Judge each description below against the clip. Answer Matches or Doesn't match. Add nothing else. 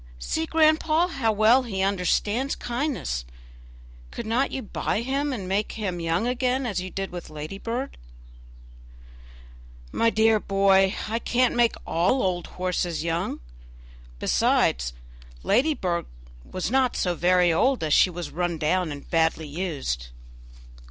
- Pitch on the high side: Matches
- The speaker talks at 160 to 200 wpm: Doesn't match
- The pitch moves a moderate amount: Doesn't match